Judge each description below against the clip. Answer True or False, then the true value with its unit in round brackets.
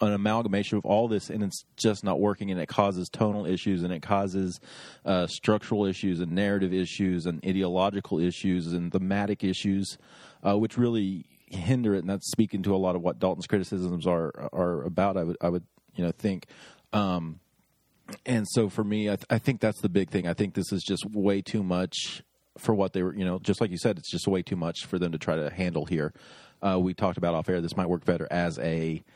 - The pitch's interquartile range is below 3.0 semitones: True (2.4 semitones)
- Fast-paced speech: True (225 wpm)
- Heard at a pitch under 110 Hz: True (95 Hz)